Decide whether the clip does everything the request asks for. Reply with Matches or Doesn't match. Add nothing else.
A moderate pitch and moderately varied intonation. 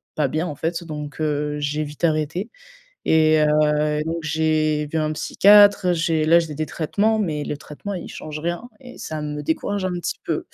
Doesn't match